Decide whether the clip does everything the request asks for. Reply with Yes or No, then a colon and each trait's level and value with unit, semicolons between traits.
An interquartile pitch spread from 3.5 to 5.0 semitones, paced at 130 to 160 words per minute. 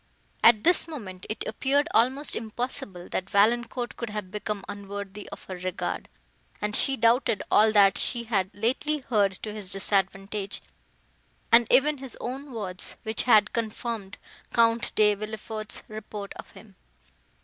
No: average, 3.0 semitones; average, 145 wpm